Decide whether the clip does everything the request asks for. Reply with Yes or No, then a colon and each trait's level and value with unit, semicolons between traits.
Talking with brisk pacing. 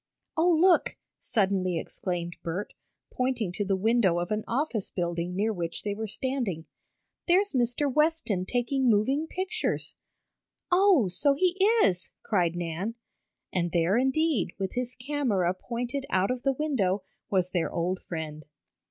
No: average, 145 wpm